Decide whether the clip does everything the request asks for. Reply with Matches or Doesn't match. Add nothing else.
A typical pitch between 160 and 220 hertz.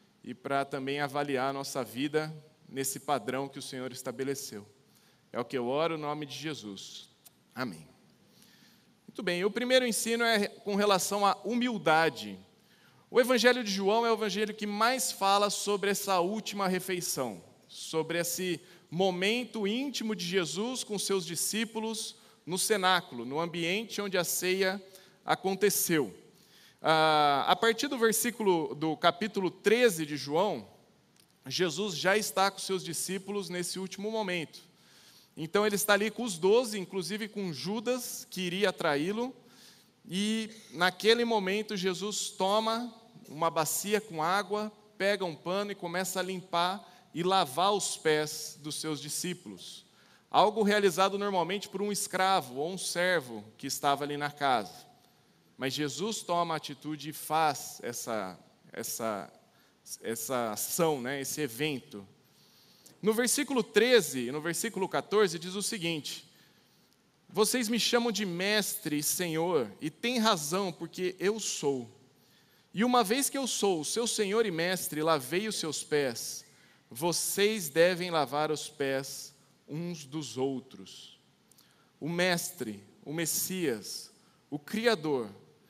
Matches